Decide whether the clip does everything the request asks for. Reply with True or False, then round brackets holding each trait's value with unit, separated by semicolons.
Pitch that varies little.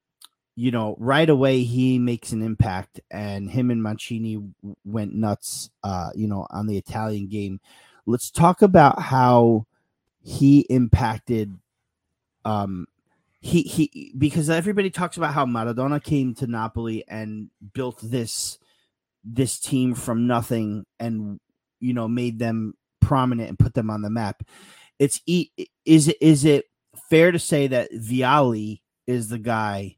False (4.1 semitones)